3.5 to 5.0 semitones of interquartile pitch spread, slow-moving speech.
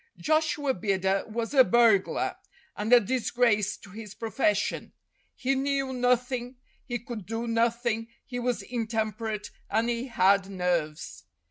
No: average, 3.0 semitones; slow, 130 wpm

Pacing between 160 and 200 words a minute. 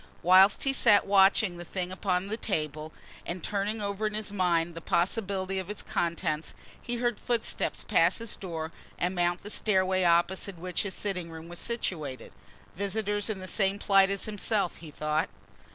Yes: average, 175 wpm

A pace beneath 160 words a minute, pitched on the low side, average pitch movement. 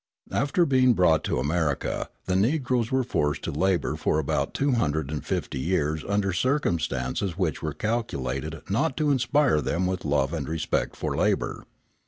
No: average, 150 wpm; very low, 90 Hz; wide, 8.4 semitones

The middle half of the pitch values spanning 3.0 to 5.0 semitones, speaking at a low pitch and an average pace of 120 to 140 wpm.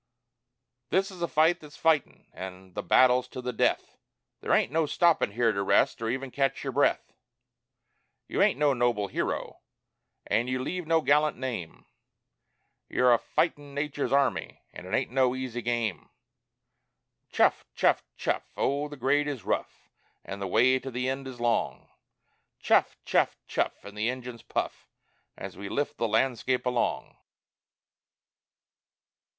No: average, 3.5 semitones; low, 130 Hz; average, 155 wpm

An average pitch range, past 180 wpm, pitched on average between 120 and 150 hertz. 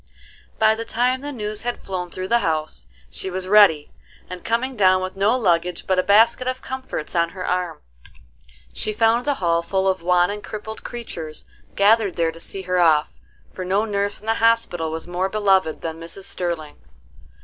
No: average, 4.1 semitones; average, 190 wpm; high, 190 Hz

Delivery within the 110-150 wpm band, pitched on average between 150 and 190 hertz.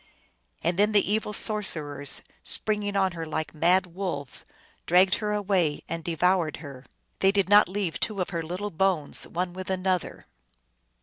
No: average, 165 wpm; medium, 185 Hz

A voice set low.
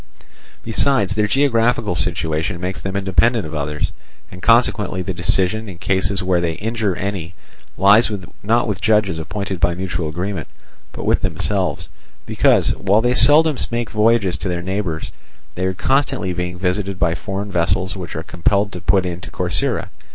Yes: very low, 95 Hz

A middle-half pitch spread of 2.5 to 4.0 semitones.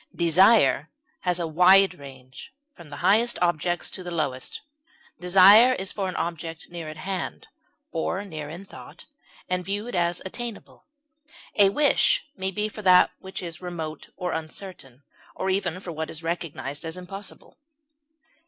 Yes: average, 3.3 semitones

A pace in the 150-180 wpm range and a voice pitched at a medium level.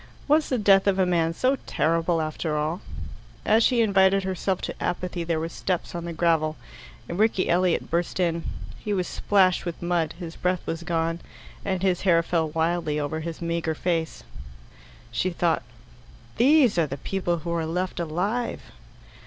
Yes: average, 170 wpm; medium, 175 Hz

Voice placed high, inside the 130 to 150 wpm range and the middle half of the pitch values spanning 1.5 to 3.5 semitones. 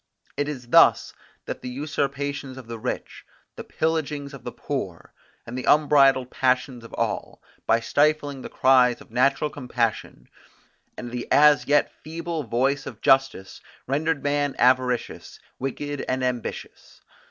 No: low, 135 Hz; average, 140 wpm; narrow, 2.6 semitones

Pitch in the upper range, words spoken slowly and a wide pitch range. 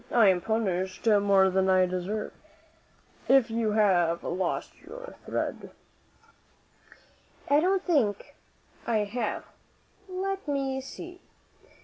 Yes: high, 220 Hz; slow, 105 wpm; wide, 6.5 semitones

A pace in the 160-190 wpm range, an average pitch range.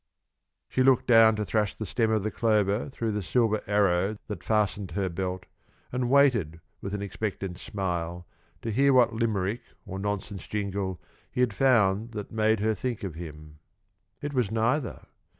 Yes: average, 170 wpm; average, 3.0 semitones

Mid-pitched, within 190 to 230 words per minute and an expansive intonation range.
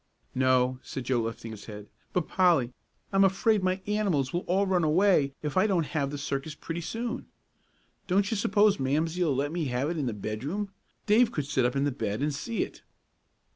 Yes: medium, 155 Hz; average, 200 wpm; wide, 6.4 semitones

